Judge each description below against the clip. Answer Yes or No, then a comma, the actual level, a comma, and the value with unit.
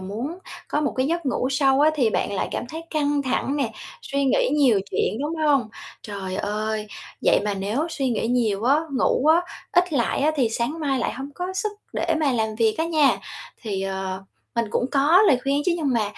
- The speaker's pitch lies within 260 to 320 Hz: Yes, very high, 265 Hz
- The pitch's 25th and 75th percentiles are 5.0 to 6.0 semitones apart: Yes, average, 5.3 semitones